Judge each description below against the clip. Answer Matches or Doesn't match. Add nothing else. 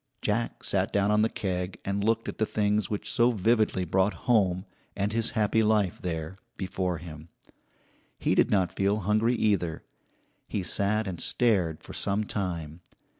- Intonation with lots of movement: Doesn't match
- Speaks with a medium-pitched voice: Doesn't match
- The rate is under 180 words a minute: Matches